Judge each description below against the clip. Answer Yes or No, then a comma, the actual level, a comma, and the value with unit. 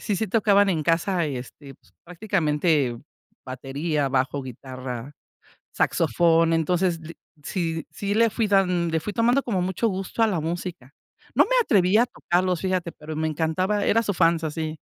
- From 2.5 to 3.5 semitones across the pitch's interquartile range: No, average, 4.1 semitones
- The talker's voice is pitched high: No, medium, 170 Hz